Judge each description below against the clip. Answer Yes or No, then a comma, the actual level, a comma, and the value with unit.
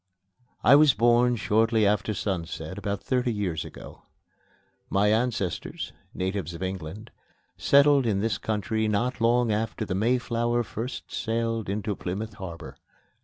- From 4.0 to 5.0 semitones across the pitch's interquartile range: No, average, 3.2 semitones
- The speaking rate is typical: No, slow, 130 wpm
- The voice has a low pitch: Yes, low, 110 Hz